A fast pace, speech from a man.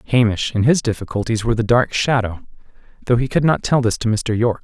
Yes: fast, 220 wpm; male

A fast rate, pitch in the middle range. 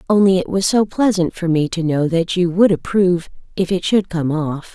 Yes: fast, 230 wpm; medium, 180 Hz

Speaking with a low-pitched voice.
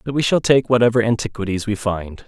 Yes: low, 115 Hz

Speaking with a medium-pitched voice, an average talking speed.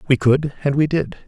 No: medium, 145 Hz; fast, 235 wpm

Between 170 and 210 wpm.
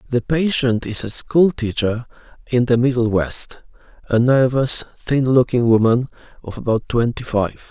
No: average, 150 wpm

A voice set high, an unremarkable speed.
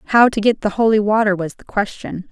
No: high, 210 Hz; fast, 235 wpm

